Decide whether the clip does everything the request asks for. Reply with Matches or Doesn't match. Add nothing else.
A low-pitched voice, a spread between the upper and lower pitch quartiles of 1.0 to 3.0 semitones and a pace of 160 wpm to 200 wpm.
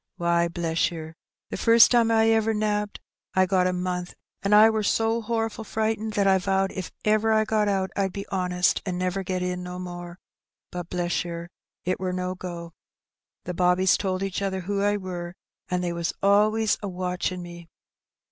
Doesn't match